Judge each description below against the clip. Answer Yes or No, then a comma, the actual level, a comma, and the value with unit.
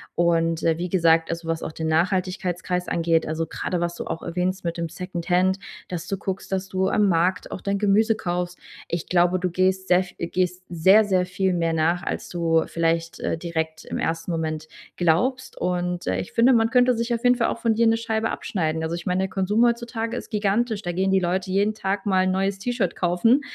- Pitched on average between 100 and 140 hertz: No, medium, 180 Hz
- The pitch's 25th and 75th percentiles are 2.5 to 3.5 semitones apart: Yes, average, 2.9 semitones